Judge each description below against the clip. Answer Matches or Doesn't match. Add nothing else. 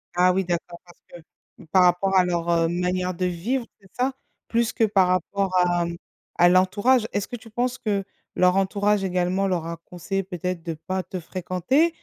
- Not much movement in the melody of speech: Matches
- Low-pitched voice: Doesn't match